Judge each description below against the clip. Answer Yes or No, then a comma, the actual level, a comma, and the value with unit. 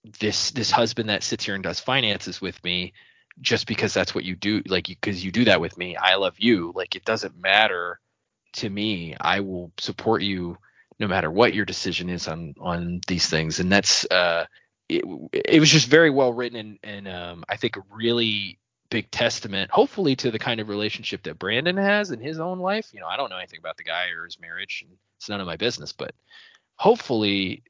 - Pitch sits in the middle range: No, low, 105 Hz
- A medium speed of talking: No, fast, 215 wpm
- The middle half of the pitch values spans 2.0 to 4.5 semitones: No, average, 4.9 semitones